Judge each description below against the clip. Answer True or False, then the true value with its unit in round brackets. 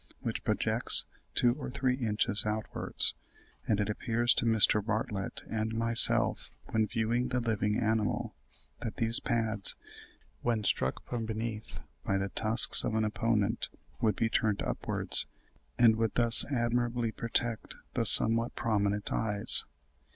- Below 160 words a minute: True (140 wpm)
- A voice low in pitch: True (110 Hz)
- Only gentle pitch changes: True (1.6 semitones)